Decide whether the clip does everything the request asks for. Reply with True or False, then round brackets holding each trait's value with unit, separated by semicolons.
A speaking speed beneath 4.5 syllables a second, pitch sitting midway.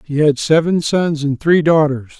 True (4.3 syllables/s; 155 Hz)